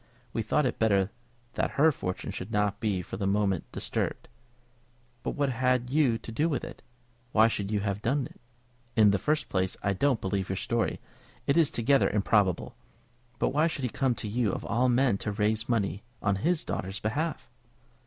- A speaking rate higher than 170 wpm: Yes, average, 195 wpm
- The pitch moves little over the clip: No, average, 4.8 semitones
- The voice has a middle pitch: No, low, 110 Hz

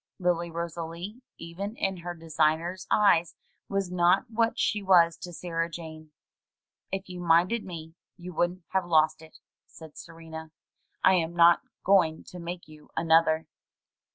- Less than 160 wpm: Yes, average, 150 wpm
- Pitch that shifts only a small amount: Yes, narrow, 2.0 semitones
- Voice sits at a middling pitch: Yes, medium, 170 Hz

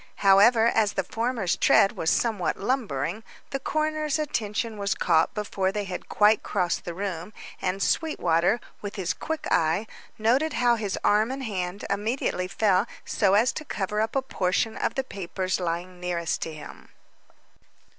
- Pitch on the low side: No, high, 205 Hz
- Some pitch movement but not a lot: Yes, average, 4.1 semitones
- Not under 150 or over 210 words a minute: Yes, average, 160 wpm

